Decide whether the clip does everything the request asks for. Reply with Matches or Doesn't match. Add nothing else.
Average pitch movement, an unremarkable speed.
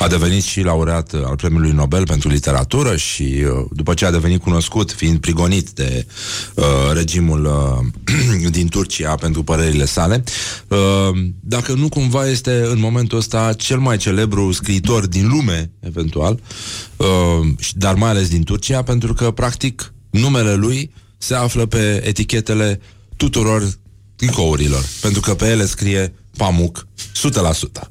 Matches